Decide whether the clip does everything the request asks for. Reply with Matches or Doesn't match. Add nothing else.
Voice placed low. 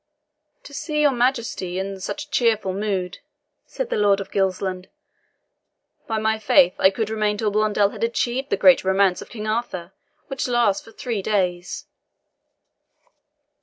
Doesn't match